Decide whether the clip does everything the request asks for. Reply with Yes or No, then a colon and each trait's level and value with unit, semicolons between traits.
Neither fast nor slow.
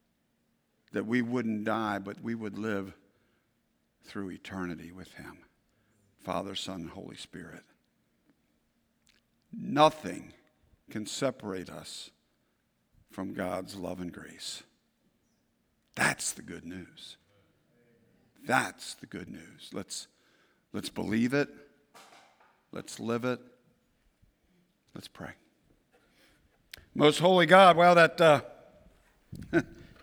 No: slow, 100 wpm